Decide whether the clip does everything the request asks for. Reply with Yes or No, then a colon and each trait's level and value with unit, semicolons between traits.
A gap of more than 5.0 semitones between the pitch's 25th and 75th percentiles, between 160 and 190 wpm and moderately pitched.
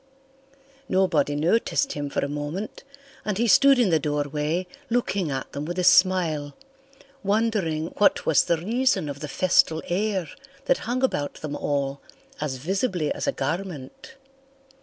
No: wide, 5.4 semitones; average, 150 wpm; medium, 170 Hz